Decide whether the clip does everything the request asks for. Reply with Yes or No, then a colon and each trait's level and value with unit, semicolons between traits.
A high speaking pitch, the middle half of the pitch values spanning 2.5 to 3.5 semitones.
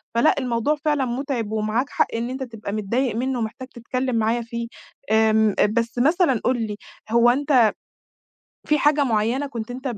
Yes: high, 240 Hz; average, 2.9 semitones